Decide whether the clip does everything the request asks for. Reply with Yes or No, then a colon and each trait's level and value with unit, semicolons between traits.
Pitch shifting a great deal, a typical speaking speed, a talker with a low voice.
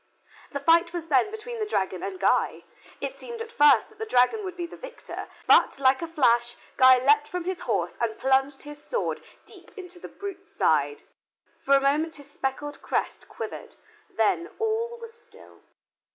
No: wide, 7.8 semitones; average, 180 wpm; very high, 335 Hz